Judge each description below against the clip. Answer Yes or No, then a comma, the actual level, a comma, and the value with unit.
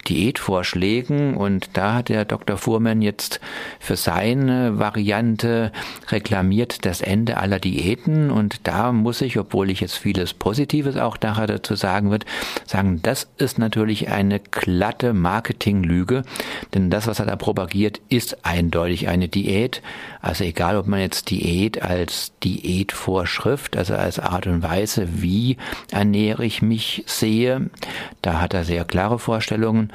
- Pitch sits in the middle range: No, low, 105 Hz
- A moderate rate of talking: Yes, average, 140 wpm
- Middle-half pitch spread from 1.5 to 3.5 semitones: Yes, average, 3.2 semitones